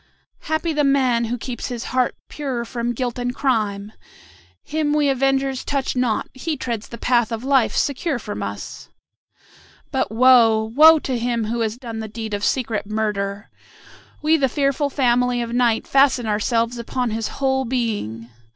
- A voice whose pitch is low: No, high, 245 Hz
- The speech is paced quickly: No, average, 165 wpm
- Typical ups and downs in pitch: Yes, average, 3.1 semitones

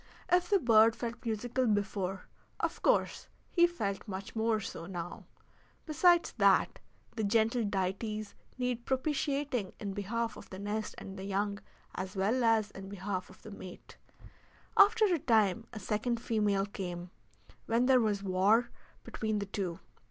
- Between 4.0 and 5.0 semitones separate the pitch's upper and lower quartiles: No, average, 3.5 semitones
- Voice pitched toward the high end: Yes, high, 215 Hz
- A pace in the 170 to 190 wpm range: No, average, 150 wpm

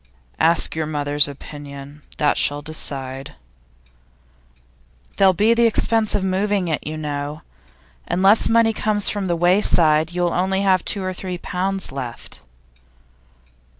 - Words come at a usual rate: No, slow, 130 wpm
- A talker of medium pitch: Yes, medium, 175 Hz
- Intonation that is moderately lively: Yes, average, 4.7 semitones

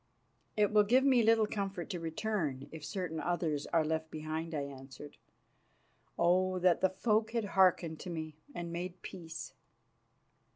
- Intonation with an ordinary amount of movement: Yes, average, 4.0 semitones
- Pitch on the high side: No, medium, 175 Hz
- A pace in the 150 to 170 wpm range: Yes, average, 155 wpm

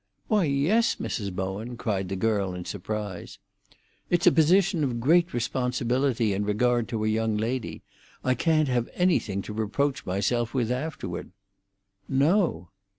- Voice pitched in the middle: No, low, 120 Hz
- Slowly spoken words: No, average, 145 wpm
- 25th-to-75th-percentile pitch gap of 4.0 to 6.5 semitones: Yes, wide, 5.4 semitones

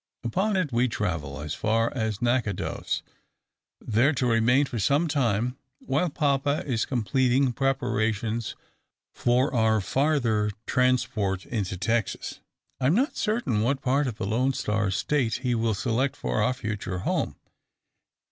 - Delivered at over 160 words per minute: No, average, 140 wpm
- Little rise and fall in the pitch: No, average, 3.9 semitones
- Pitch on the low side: Yes, low, 120 Hz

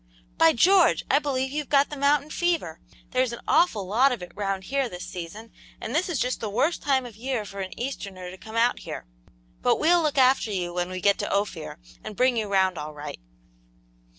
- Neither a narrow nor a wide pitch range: No, wide, 6.6 semitones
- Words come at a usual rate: No, fast, 215 wpm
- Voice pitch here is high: Yes, high, 230 Hz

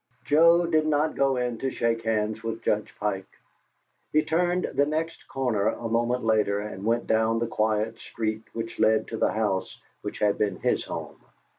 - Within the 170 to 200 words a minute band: Yes, average, 180 wpm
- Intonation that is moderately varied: Yes, average, 4.2 semitones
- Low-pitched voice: Yes, low, 115 Hz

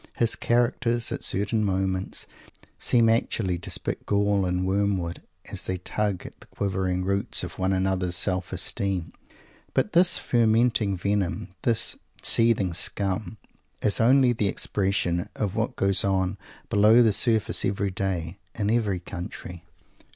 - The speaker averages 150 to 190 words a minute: No, average, 140 wpm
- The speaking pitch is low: Yes, low, 100 Hz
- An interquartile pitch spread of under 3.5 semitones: Yes, average, 3.0 semitones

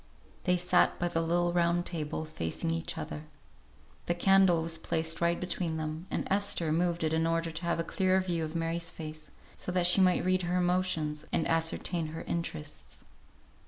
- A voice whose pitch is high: No, medium, 170 Hz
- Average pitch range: No, narrow, 1.7 semitones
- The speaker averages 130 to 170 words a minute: No, average, 185 wpm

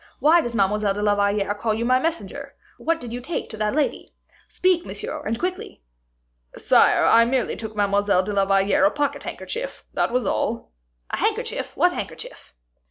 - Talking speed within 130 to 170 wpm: No, average, 180 wpm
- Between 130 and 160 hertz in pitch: No, high, 225 Hz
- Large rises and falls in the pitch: Yes, wide, 5.8 semitones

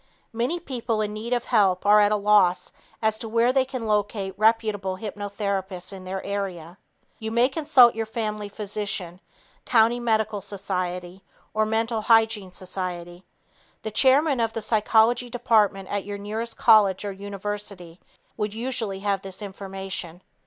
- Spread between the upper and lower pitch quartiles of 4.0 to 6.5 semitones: No, average, 2.7 semitones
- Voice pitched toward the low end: No, high, 210 Hz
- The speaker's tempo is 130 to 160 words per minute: Yes, average, 150 wpm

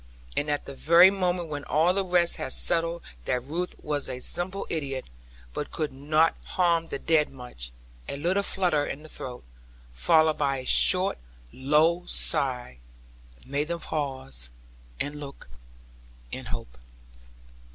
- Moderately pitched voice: Yes, medium, 150 Hz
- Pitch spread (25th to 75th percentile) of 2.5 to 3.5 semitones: No, average, 4.0 semitones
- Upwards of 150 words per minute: No, average, 145 wpm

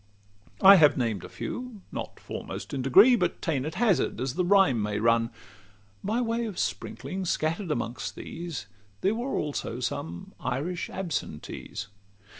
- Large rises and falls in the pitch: Yes, wide, 8.0 semitones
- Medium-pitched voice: Yes, medium, 165 Hz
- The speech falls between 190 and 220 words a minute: No, average, 150 wpm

